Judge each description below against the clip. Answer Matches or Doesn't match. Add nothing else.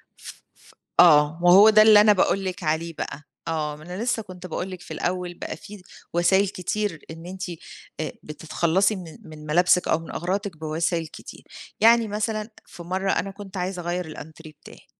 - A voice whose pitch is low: Doesn't match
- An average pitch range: Matches